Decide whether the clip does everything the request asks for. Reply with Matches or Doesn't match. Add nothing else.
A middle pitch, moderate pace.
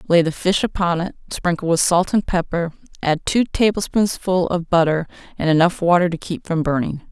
Matches